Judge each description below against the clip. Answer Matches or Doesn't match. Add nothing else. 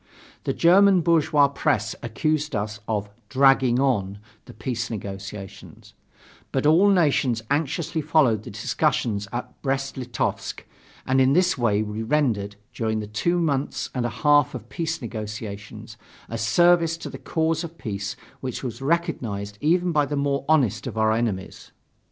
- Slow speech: Doesn't match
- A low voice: Matches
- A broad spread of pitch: Matches